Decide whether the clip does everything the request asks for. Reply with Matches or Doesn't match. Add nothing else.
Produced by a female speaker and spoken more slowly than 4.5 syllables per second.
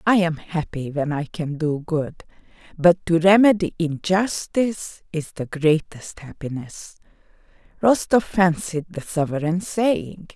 Matches